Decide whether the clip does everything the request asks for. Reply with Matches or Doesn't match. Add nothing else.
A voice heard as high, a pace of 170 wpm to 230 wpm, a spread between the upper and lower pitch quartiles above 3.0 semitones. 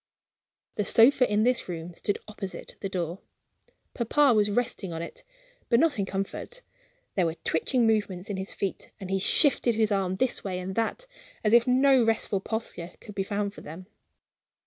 Matches